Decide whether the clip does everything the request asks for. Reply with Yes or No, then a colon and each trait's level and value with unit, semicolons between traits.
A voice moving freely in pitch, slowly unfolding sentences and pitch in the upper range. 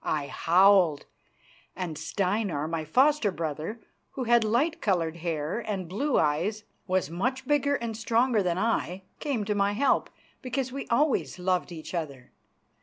No: wide, 6.0 semitones; average, 155 wpm; high, 200 Hz